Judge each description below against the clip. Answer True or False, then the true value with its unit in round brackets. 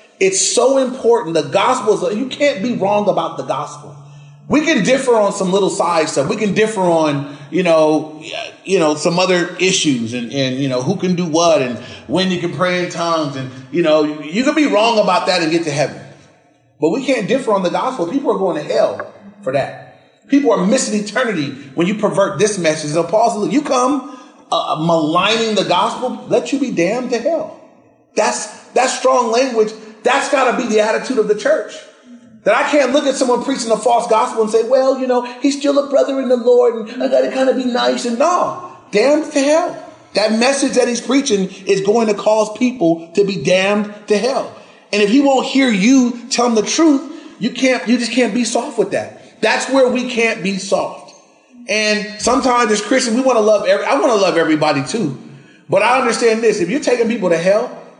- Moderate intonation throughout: False (5.8 semitones)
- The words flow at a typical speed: False (215 wpm)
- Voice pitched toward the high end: True (220 Hz)